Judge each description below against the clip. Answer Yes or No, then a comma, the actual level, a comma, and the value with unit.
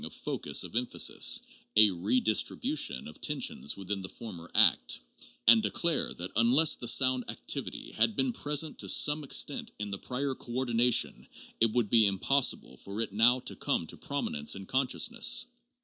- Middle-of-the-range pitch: No, low, 115 Hz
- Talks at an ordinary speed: Yes, average, 165 wpm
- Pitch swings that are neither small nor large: Yes, average, 4.7 semitones